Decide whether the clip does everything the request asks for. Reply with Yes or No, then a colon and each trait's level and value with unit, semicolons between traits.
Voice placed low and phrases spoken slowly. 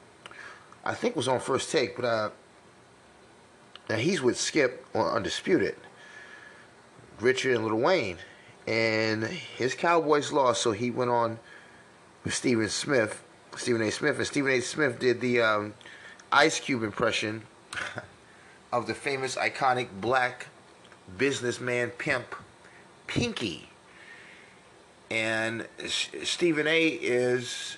Yes: low, 120 Hz; slow, 115 wpm